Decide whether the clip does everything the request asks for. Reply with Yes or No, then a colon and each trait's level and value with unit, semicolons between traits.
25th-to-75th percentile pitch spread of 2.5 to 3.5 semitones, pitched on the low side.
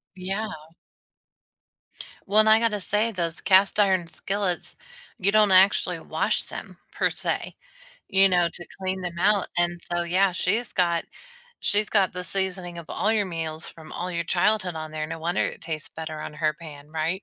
No: average, 2.8 semitones; medium, 180 Hz